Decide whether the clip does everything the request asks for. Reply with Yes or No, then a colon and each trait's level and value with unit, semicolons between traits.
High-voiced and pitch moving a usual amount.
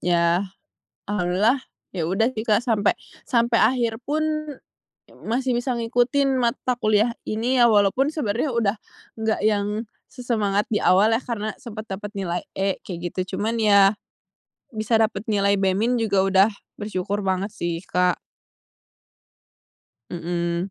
Yes: high, 210 Hz; average, 3.4 semitones